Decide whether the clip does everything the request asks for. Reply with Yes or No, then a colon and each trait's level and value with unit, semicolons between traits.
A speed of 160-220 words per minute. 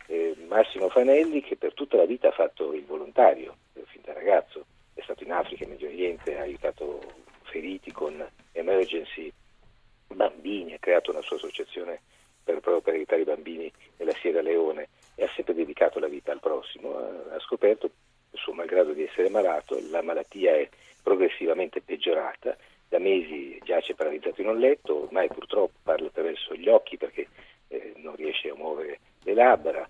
Yes: average, 165 wpm